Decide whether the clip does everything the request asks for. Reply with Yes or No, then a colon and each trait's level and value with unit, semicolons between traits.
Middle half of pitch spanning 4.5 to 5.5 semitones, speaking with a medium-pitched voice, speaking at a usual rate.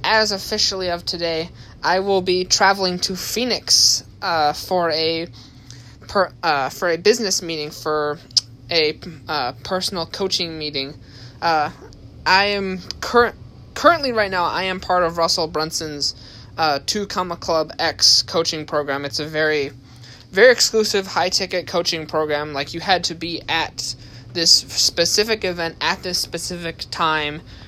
Yes: average, 5.0 semitones; medium, 165 Hz; average, 145 wpm